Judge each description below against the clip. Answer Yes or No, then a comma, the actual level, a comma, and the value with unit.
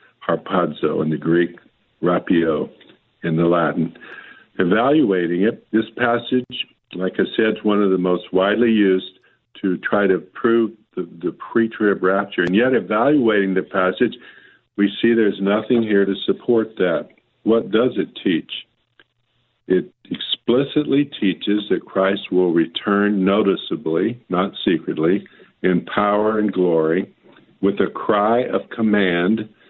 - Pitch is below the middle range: Yes, low, 100 Hz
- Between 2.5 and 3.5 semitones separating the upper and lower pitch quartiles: Yes, average, 3.2 semitones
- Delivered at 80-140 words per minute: Yes, slow, 135 wpm